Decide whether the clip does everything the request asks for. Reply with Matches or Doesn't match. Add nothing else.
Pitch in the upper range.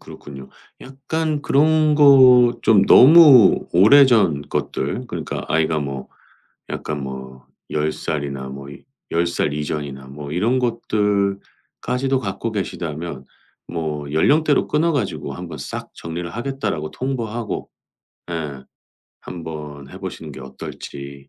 Doesn't match